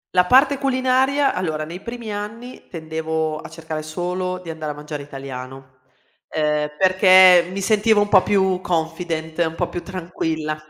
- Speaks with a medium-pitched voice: Yes, medium, 175 Hz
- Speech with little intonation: No, average, 4.3 semitones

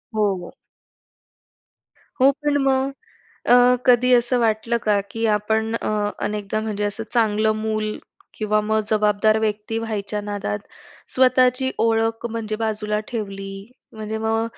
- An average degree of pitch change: No, narrow, 1.5 semitones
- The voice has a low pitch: No, high, 220 Hz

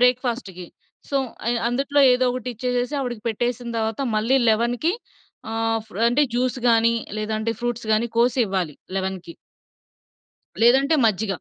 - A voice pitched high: Yes, high, 235 Hz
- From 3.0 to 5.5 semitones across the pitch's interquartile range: No, narrow, 2.4 semitones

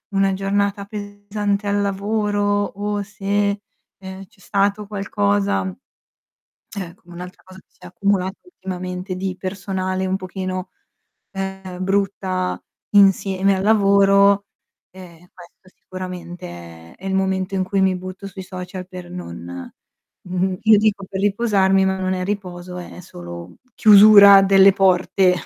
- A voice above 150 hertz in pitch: Yes, high, 190 Hz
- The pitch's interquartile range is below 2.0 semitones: Yes, narrow, 1.6 semitones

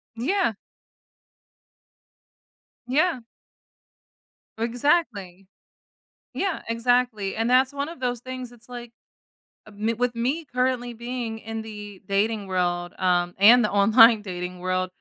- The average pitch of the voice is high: Yes, high, 230 Hz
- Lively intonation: No, average, 3.9 semitones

